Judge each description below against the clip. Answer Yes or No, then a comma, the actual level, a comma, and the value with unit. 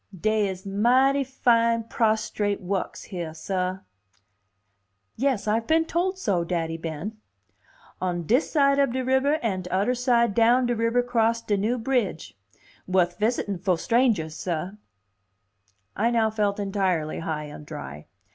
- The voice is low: No, high, 215 Hz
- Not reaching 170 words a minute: Yes, average, 140 wpm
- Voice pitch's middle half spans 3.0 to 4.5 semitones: No, average, 5.0 semitones